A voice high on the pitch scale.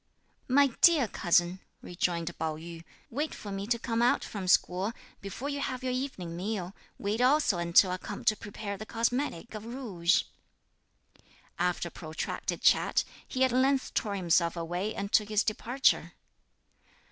Yes: high, 205 Hz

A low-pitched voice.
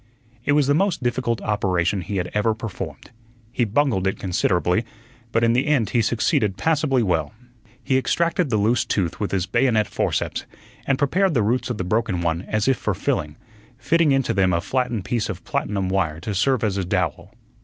Yes: low, 110 Hz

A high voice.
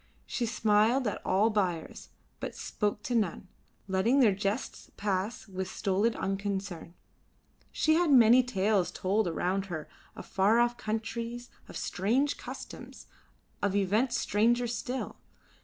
Yes: high, 210 Hz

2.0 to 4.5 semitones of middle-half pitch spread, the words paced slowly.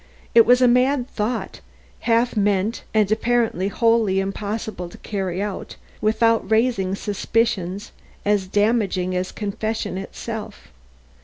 Yes: average, 3.0 semitones; slow, 120 wpm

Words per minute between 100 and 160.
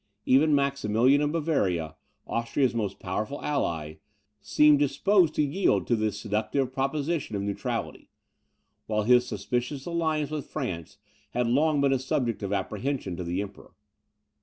Yes: average, 140 wpm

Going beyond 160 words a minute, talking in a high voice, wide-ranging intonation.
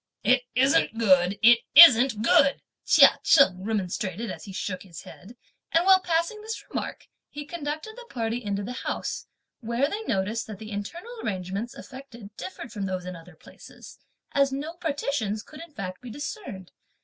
Yes: average, 170 wpm; high, 235 Hz; wide, 6.7 semitones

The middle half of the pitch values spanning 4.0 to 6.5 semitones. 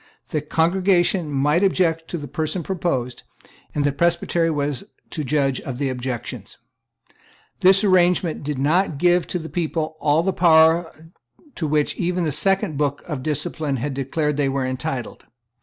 No: average, 3.6 semitones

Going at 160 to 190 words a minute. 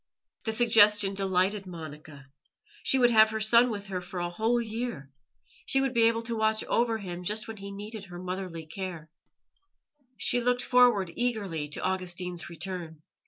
Yes: average, 165 wpm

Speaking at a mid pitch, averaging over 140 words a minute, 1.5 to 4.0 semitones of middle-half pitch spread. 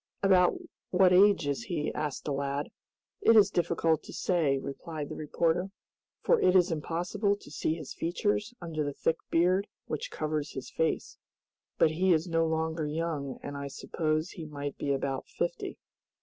Yes: medium, 160 Hz; average, 170 wpm; average, 3.4 semitones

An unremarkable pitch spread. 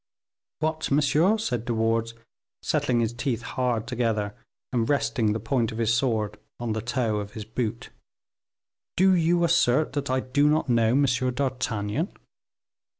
Yes: average, 4.0 semitones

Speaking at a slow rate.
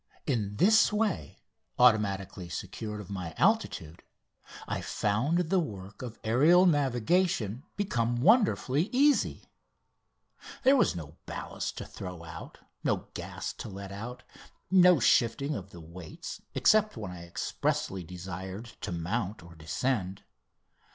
Yes: slow, 125 wpm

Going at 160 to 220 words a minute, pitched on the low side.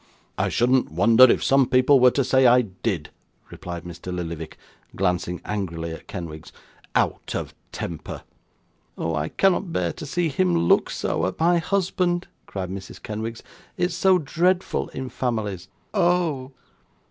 No: average, 145 wpm; low, 115 Hz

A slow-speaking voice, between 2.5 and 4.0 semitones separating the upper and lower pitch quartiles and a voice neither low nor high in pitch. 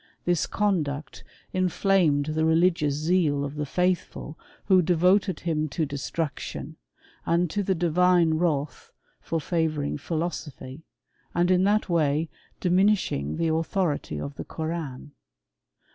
Yes: slow, 125 wpm; average, 3.4 semitones; medium, 165 Hz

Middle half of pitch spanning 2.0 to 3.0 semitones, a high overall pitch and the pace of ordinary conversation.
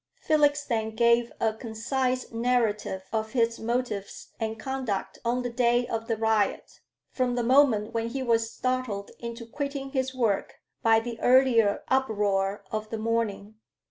Yes: narrow, 2.5 semitones; high, 230 Hz; average, 150 wpm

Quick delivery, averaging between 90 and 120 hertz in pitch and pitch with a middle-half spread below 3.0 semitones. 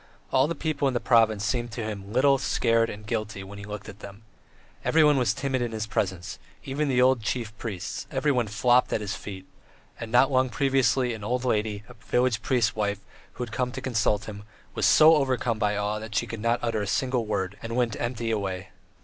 No: fast, 215 wpm; low, 115 Hz; average, 3.4 semitones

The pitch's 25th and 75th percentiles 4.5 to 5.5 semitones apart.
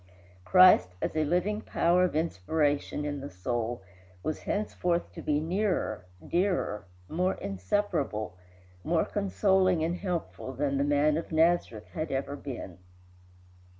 Yes: average, 5.2 semitones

